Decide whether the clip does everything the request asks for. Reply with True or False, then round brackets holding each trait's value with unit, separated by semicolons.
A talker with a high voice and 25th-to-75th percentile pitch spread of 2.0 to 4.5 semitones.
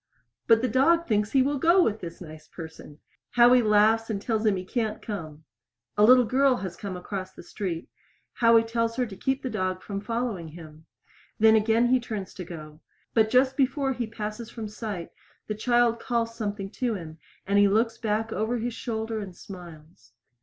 True (220 Hz; 4.1 semitones)